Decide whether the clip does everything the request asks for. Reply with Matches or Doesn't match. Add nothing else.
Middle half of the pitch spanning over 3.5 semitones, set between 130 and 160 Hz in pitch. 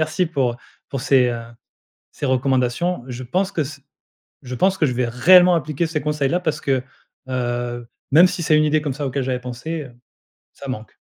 Matches